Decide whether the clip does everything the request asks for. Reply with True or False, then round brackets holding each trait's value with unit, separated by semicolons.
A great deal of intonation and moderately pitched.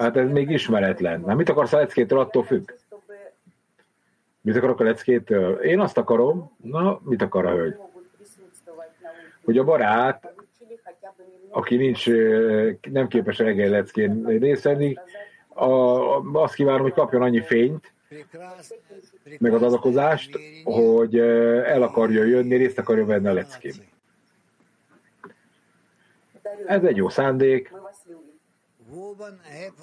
True (8.1 semitones; 145 Hz)